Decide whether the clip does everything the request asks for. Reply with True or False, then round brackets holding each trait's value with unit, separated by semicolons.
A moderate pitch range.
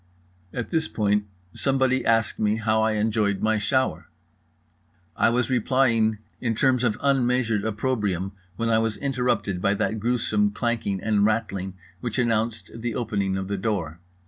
True (3.0 semitones)